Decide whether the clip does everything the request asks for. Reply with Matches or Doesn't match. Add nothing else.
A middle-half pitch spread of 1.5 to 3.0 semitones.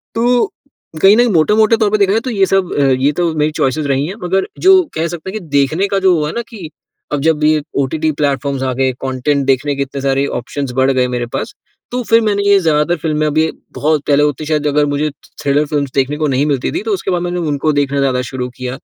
Doesn't match